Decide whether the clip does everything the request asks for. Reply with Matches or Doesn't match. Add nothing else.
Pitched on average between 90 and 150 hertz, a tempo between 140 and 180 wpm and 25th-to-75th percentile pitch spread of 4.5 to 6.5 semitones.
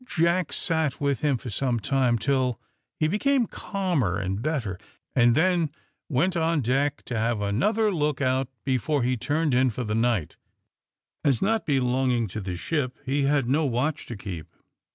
Matches